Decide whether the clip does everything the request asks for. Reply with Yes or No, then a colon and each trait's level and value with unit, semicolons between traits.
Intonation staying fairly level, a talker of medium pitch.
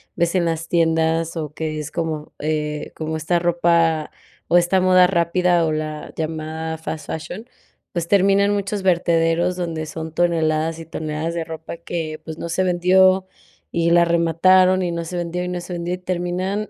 Yes: narrow, 1.9 semitones; medium, 170 Hz